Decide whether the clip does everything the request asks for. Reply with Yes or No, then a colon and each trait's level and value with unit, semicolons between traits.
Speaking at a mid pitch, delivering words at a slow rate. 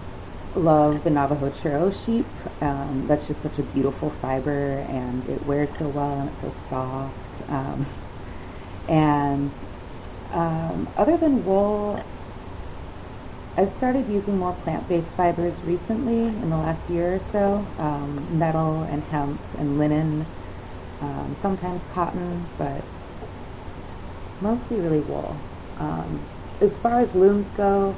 Yes: medium, 150 Hz; slow, 130 wpm